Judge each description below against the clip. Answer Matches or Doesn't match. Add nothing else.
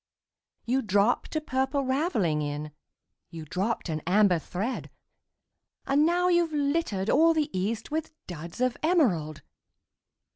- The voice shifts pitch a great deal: Matches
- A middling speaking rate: Doesn't match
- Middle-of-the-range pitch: Doesn't match